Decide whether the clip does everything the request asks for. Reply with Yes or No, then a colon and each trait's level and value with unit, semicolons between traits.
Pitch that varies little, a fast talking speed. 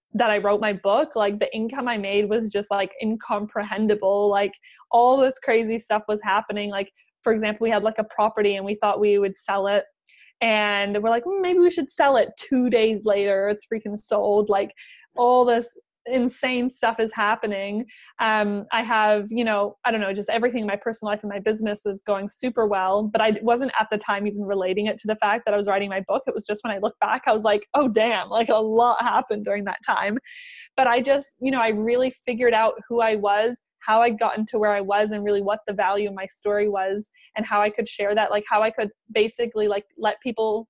Yes: narrow, 2.3 semitones; fast, 230 wpm